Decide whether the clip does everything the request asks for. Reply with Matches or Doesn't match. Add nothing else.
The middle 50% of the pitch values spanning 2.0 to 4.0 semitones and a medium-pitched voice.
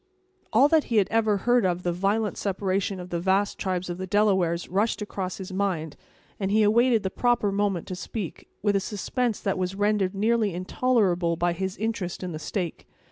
Doesn't match